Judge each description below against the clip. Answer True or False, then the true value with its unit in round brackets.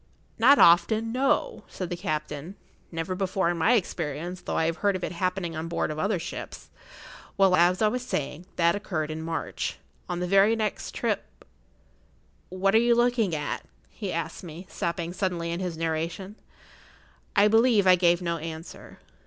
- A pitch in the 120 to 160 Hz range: False (180 Hz)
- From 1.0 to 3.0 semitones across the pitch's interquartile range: False (3.4 semitones)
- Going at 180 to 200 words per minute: False (170 wpm)